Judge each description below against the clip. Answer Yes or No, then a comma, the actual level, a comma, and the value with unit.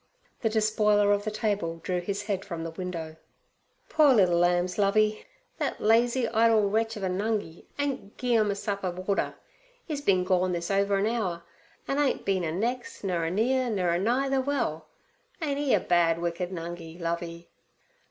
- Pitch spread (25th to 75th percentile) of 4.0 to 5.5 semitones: Yes, average, 4.4 semitones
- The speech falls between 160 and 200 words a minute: Yes, average, 185 wpm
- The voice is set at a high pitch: Yes, high, 200 Hz